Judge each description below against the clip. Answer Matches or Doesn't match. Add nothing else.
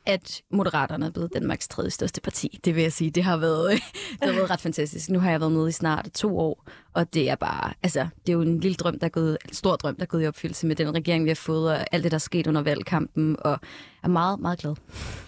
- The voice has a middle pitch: Matches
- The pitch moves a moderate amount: Doesn't match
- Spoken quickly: Matches